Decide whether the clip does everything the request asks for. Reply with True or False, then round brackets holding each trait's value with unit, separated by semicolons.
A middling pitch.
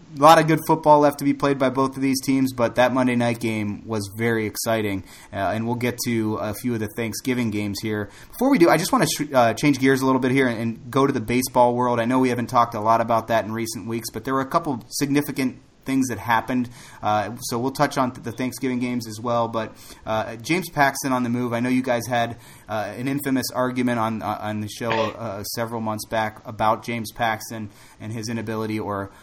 False (120 Hz)